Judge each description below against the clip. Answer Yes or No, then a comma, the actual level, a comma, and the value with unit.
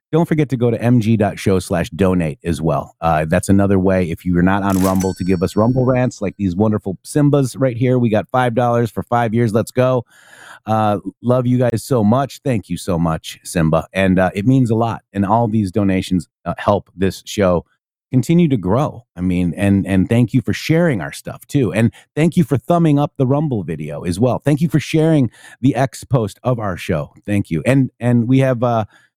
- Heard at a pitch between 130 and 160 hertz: No, low, 115 Hz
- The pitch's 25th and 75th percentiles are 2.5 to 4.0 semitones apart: No, average, 5.3 semitones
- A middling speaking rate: No, fast, 220 wpm